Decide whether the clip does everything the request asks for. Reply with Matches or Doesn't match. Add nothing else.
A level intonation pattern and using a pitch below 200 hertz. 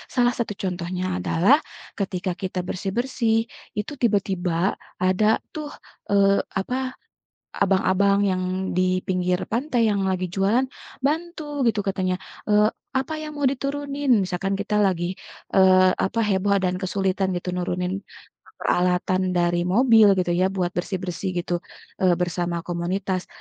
Doesn't match